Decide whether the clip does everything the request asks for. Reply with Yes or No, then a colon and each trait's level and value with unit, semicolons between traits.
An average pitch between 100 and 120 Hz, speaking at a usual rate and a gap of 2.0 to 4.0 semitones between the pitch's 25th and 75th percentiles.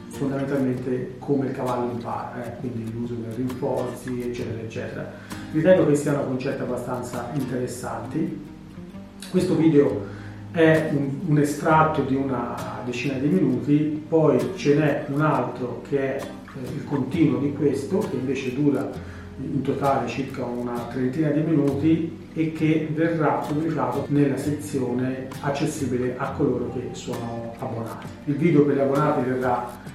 No: low, 135 Hz; average, 135 wpm; average, 3.2 semitones